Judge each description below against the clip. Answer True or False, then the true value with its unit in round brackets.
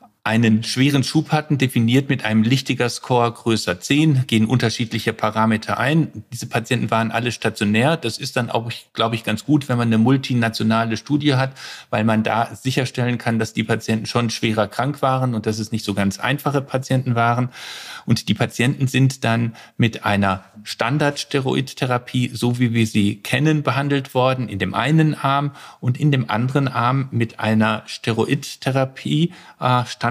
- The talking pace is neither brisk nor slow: True (165 wpm)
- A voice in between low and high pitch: False (120 Hz)